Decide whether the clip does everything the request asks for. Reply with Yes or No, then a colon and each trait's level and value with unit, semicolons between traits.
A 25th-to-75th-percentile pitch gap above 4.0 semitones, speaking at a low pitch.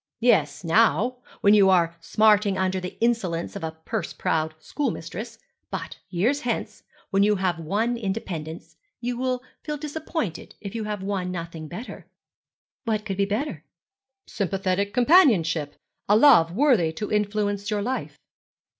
No: average, 5.0 semitones; high, 200 Hz